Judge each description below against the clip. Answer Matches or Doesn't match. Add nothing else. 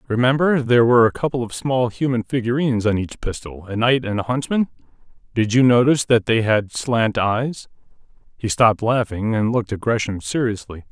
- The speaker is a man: Matches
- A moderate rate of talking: Matches